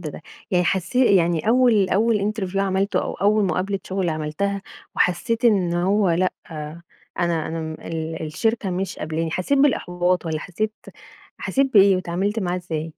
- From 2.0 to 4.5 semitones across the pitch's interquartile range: Yes, average, 3.3 semitones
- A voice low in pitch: No, medium, 185 Hz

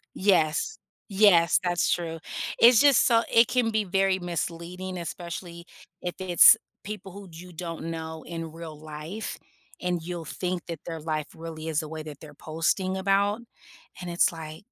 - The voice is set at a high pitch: No, medium, 175 Hz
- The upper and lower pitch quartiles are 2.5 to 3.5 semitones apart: Yes, average, 2.9 semitones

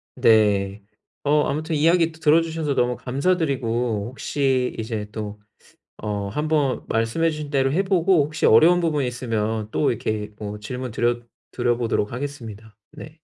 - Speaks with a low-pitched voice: Yes, low, 125 Hz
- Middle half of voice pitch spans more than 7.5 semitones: No, wide, 5.6 semitones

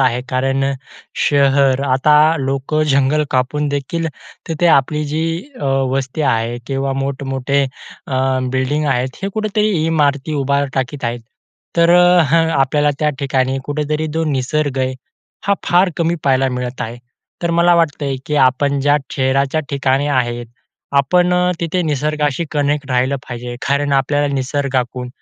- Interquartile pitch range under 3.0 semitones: Yes, narrow, 2.5 semitones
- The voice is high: No, medium, 140 Hz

